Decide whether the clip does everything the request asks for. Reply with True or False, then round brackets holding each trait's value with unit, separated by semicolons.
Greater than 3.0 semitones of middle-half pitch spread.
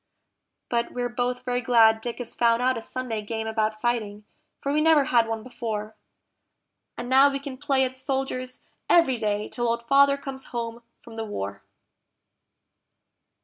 False (2.7 semitones)